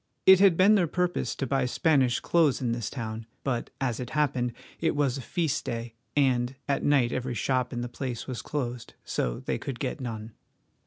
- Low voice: Yes, low, 130 Hz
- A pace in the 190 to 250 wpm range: Yes, average, 200 wpm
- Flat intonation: No, average, 3.3 semitones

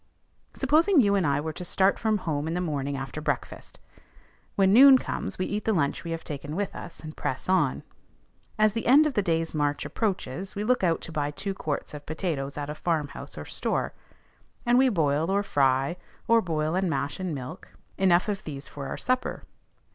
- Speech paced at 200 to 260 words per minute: Yes, fast, 205 wpm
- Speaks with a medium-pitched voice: Yes, medium, 170 Hz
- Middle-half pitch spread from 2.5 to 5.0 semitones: No, wide, 5.6 semitones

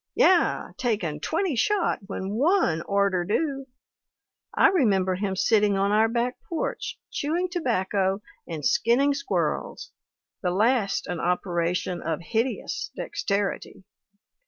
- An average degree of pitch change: No, wide, 6.6 semitones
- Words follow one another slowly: Yes, slow, 115 wpm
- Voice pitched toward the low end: No, high, 210 Hz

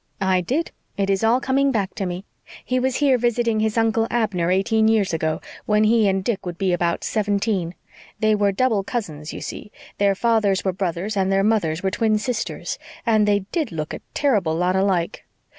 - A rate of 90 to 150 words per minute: No, average, 195 wpm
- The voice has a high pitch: Yes, high, 205 Hz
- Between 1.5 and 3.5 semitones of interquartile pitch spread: Yes, average, 3.1 semitones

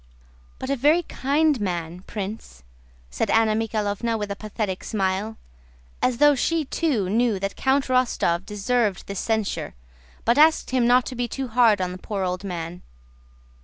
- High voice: Yes, high, 220 Hz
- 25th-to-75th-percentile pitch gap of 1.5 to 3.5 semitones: No, average, 4.7 semitones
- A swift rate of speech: No, average, 165 wpm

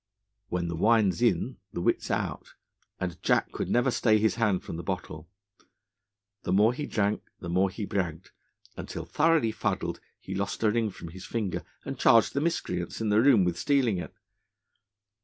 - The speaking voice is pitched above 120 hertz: No, low, 105 Hz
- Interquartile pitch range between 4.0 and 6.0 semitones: Yes, average, 4.4 semitones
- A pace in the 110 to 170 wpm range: No, average, 185 wpm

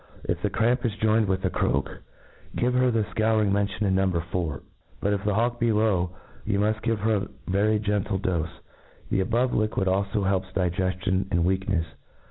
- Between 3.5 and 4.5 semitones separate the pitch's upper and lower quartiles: No, narrow, 2.6 semitones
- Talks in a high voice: No, low, 100 Hz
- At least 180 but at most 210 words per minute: Yes, average, 190 wpm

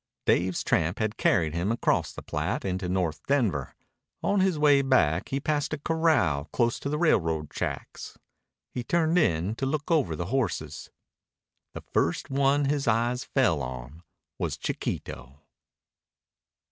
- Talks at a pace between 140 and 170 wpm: Yes, average, 145 wpm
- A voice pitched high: No, low, 115 Hz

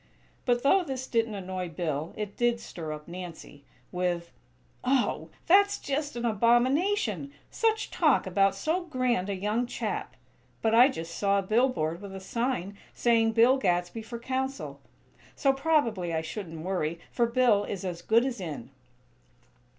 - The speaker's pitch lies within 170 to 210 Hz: No, high, 220 Hz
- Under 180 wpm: Yes, average, 155 wpm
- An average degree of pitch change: No, wide, 6.1 semitones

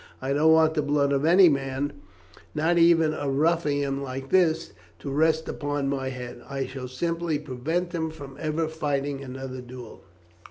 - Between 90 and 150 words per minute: No, average, 170 wpm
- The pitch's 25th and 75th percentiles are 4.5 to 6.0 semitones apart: No, average, 2.9 semitones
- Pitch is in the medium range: Yes, medium, 145 Hz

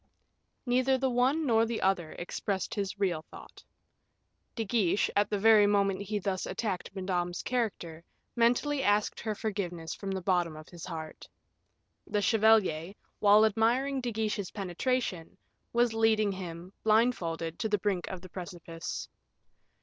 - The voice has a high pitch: Yes, high, 205 Hz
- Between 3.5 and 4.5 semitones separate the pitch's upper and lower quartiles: Yes, average, 3.9 semitones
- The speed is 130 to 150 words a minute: Yes, average, 145 wpm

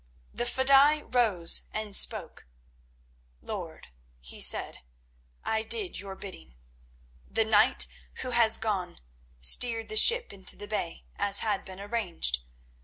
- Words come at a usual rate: No, slow, 125 wpm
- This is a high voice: Yes, high, 215 Hz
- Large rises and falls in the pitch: No, average, 4.1 semitones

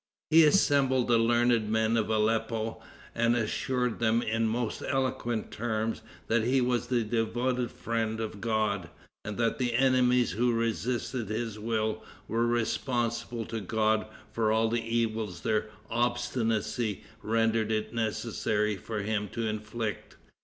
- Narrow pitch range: Yes, narrow, 1.6 semitones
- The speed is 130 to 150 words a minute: Yes, average, 140 wpm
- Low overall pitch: Yes, low, 115 Hz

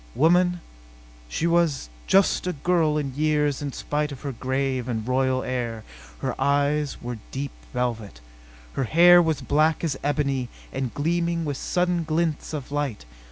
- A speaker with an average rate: Yes, average, 155 wpm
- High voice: No, medium, 145 Hz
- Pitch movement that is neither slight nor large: Yes, average, 3.8 semitones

